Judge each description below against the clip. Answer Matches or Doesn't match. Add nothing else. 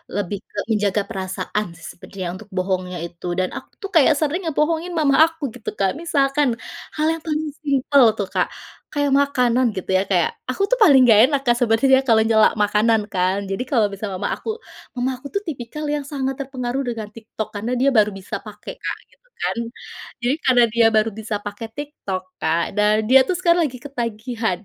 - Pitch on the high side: Matches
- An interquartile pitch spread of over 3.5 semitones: Matches